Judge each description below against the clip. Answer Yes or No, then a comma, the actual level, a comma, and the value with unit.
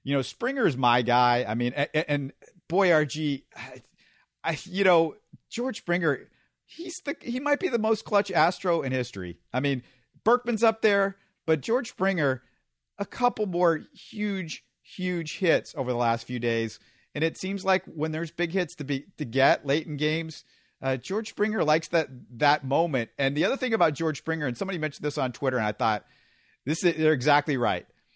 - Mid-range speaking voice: Yes, medium, 155 Hz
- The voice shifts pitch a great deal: Yes, wide, 6.3 semitones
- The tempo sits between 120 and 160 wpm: No, average, 190 wpm